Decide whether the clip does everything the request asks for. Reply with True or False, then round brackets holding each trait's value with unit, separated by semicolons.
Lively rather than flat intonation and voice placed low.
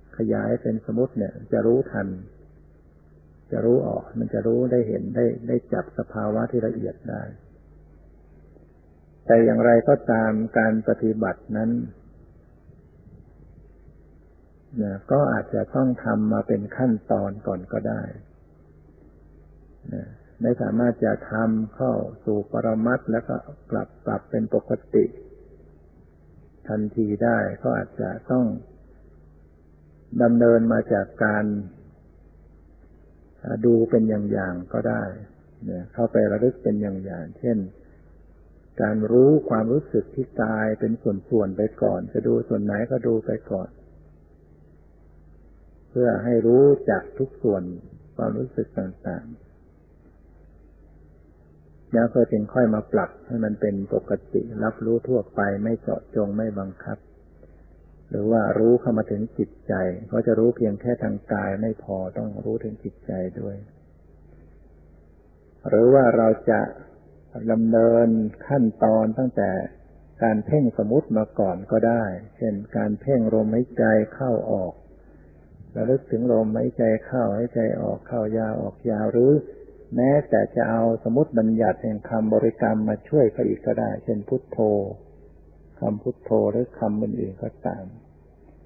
True (6.3 semitones; 105 Hz)